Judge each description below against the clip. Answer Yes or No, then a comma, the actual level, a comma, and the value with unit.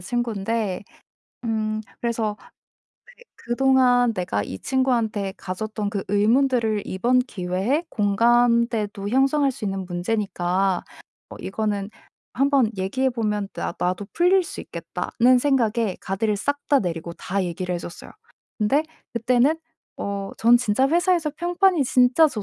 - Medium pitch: No, high, 225 Hz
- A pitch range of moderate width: Yes, average, 4.7 semitones